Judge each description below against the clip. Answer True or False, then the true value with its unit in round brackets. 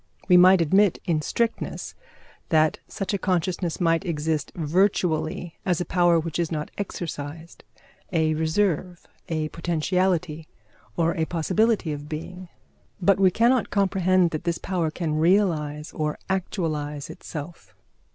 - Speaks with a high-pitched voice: False (170 Hz)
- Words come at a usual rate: False (130 wpm)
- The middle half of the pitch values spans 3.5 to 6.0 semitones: False (2.9 semitones)